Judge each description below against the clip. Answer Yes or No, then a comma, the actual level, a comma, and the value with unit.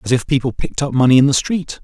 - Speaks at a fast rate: Yes, fast, 295 wpm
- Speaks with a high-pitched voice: No, low, 135 Hz